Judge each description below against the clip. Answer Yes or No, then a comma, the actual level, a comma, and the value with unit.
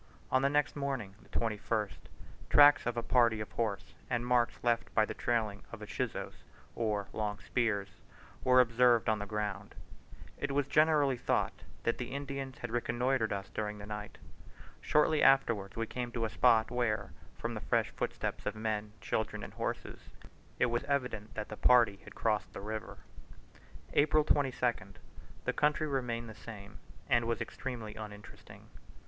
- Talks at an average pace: Yes, average, 165 wpm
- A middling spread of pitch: Yes, average, 3.0 semitones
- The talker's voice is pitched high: No, low, 115 Hz